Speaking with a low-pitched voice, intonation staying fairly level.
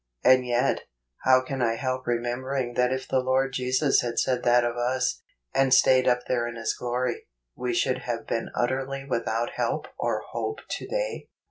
Yes: low, 125 Hz; narrow, 1.4 semitones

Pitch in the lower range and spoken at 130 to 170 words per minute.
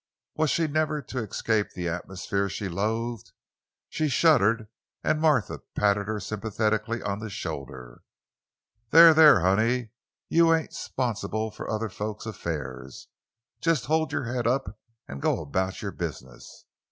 Yes: low, 110 Hz; average, 140 wpm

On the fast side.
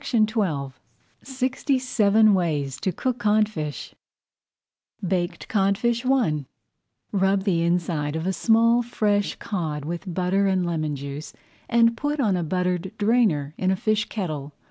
No: average, 140 wpm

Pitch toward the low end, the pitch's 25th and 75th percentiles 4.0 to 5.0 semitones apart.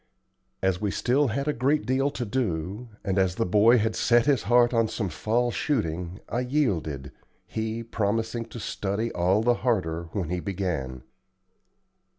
Yes: low, 110 Hz; average, 4.7 semitones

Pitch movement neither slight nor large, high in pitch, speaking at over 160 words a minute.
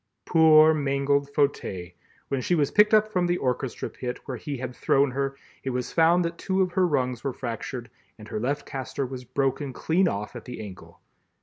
No: average, 4.3 semitones; medium, 140 Hz; average, 200 wpm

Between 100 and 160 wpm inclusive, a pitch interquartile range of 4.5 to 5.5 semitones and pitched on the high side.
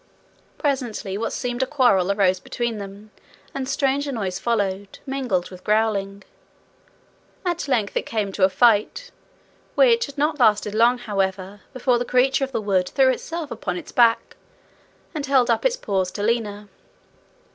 Yes: average, 155 wpm; average, 5.0 semitones; high, 230 Hz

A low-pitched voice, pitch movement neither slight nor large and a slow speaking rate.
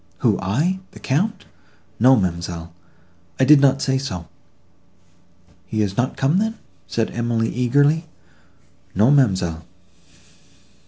No: low, 125 Hz; wide, 6.6 semitones; slow, 110 wpm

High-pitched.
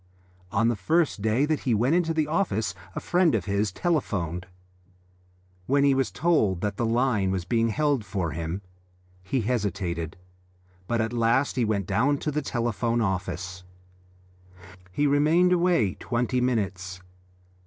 No: low, 115 Hz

